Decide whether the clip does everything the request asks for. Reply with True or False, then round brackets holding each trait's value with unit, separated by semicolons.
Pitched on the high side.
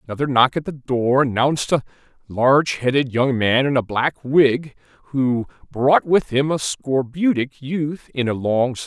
False (135 Hz)